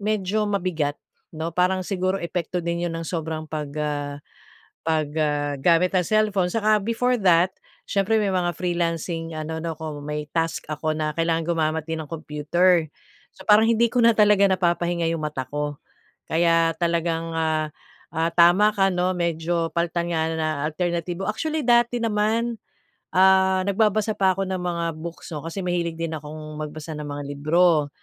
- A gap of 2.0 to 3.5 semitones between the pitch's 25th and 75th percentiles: Yes, average, 3.1 semitones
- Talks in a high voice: No, medium, 170 Hz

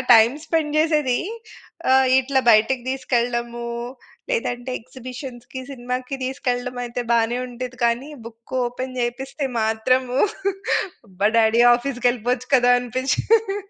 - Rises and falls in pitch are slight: Yes, narrow, 1.7 semitones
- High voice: Yes, very high, 250 Hz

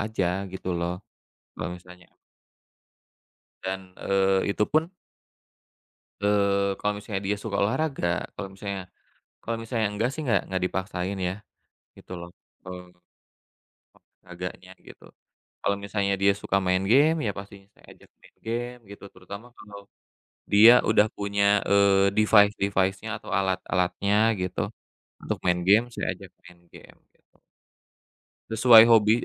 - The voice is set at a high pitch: No, low, 100 Hz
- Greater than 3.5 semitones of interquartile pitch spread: No, narrow, 2.4 semitones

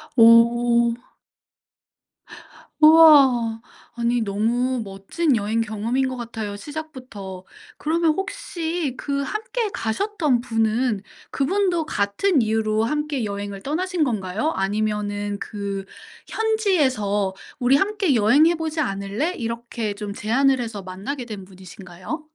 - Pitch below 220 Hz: No, high, 235 Hz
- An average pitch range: No, wide, 6.7 semitones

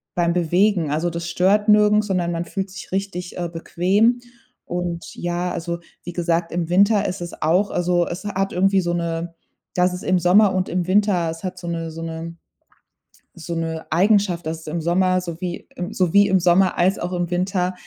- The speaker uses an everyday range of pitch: No, narrow, 2.0 semitones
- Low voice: No, medium, 180 Hz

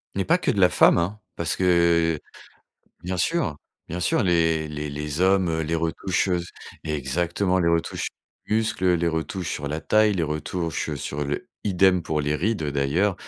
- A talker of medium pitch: No, very low, 85 Hz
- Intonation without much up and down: No, average, 3.2 semitones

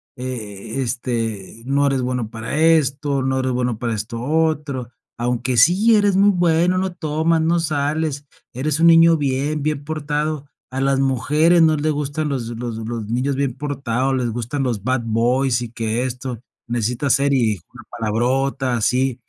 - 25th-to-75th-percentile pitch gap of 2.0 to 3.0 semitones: No, average, 4.1 semitones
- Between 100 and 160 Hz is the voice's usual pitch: Yes, low, 135 Hz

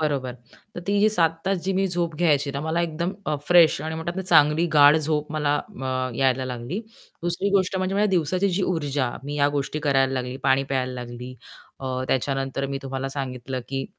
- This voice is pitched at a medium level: Yes, medium, 145 Hz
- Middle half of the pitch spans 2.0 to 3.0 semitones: No, average, 4.4 semitones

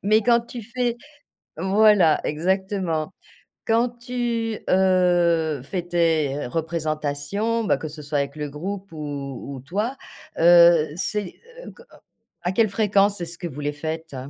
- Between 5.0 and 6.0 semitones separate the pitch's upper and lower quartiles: Yes, average, 5.3 semitones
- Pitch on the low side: No, medium, 175 Hz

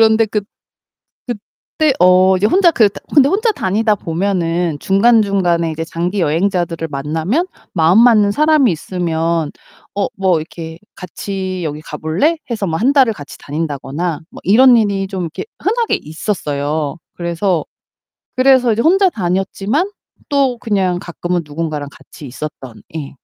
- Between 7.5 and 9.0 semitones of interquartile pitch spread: No, wide, 5.5 semitones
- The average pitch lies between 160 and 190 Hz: Yes, medium, 185 Hz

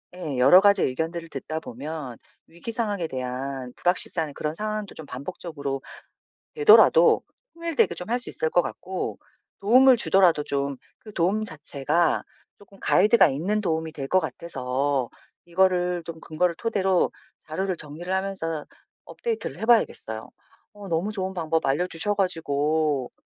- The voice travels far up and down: No, average, 4.9 semitones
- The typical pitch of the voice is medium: Yes, medium, 170 Hz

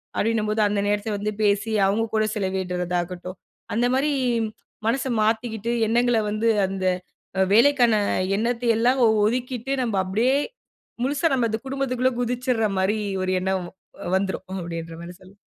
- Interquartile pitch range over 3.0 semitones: Yes, average, 4.2 semitones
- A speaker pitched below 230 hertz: Yes, high, 220 Hz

